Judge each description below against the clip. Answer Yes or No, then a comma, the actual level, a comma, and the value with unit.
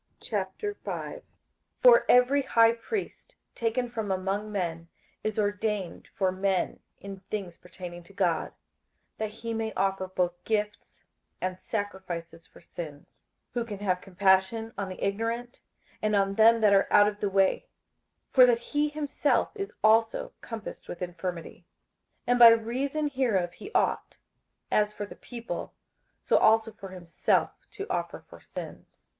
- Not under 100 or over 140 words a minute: No, average, 150 wpm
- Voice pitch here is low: No, high, 210 Hz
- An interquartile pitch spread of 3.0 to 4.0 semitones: Yes, average, 3.6 semitones